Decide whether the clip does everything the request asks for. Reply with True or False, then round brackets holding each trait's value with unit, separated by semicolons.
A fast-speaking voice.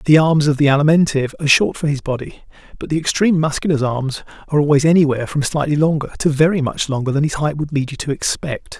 True (225 wpm)